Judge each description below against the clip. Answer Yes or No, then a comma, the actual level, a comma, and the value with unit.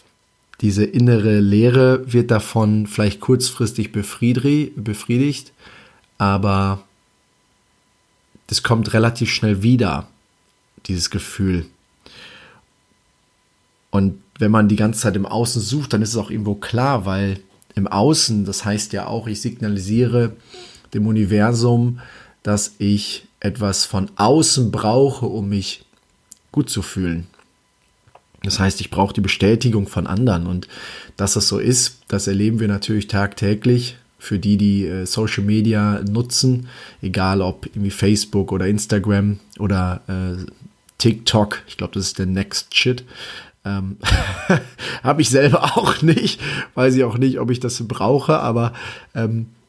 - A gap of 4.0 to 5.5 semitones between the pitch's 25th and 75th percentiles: No, average, 3.3 semitones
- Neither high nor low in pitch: No, low, 105 Hz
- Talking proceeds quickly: No, average, 135 wpm